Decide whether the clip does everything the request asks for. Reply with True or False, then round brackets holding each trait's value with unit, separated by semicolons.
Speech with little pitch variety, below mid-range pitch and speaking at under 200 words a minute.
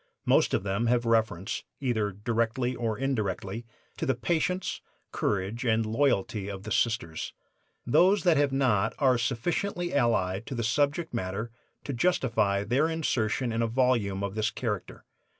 False (4.4 semitones; 115 Hz; 150 wpm)